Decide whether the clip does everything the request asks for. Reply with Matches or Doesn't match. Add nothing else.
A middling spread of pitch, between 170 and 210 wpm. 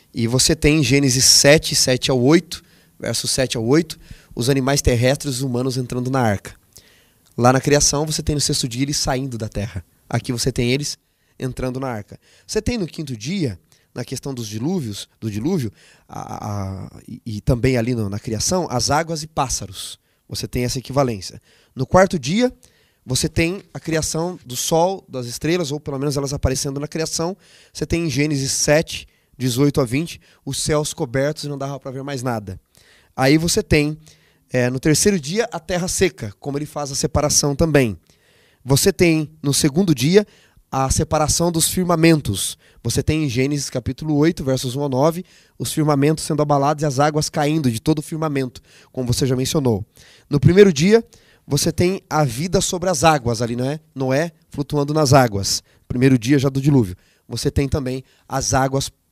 Matches